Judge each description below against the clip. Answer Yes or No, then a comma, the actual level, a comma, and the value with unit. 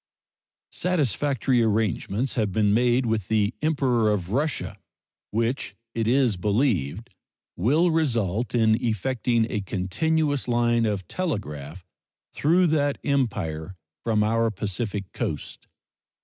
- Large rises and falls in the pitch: No, average, 4.6 semitones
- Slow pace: Yes, slow, 110 wpm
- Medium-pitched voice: No, low, 115 Hz